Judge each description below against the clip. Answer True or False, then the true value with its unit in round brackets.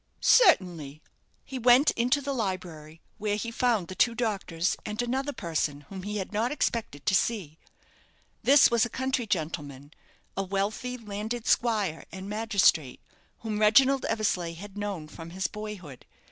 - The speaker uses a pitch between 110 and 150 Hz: False (205 Hz)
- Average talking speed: True (150 wpm)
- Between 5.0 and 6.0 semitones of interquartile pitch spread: True (5.5 semitones)